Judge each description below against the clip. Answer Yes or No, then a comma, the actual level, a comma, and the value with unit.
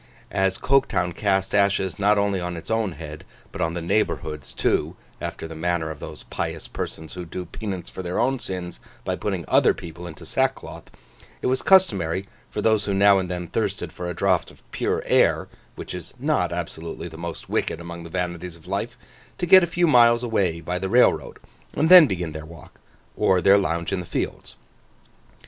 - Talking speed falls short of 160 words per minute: No, average, 190 wpm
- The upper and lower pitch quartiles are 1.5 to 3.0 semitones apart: No, average, 3.4 semitones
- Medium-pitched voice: No, very low, 90 Hz